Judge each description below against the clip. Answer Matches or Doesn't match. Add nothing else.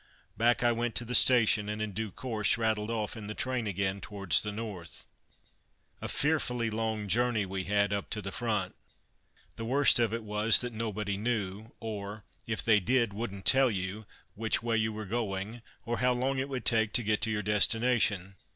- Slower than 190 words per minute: Doesn't match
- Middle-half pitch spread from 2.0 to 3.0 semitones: Matches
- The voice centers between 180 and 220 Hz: Doesn't match